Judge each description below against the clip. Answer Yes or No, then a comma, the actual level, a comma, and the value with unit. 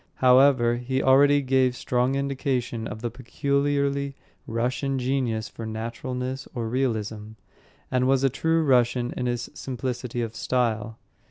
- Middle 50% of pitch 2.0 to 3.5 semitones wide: Yes, narrow, 2.4 semitones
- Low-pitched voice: Yes, low, 125 Hz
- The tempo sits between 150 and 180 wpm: No, slow, 135 wpm